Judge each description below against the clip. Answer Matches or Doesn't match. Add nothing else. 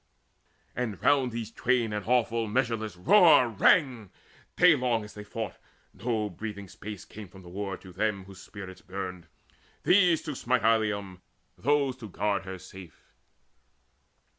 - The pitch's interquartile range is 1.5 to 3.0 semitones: Doesn't match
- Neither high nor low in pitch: Doesn't match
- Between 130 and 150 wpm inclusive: Matches